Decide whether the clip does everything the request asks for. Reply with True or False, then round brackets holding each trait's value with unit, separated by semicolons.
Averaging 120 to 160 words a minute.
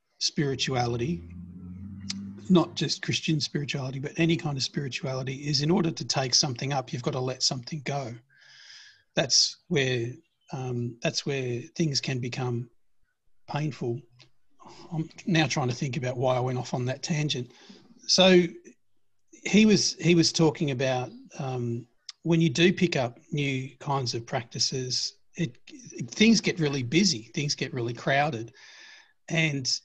True (145 wpm)